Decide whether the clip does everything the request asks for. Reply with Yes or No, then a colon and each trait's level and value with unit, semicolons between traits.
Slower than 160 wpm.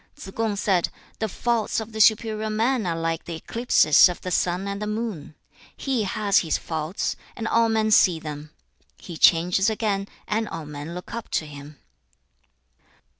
No: average, 170 wpm